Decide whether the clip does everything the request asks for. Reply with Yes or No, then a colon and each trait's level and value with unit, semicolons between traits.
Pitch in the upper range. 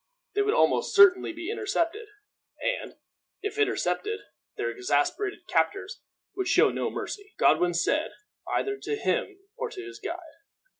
Yes: very high, 405 Hz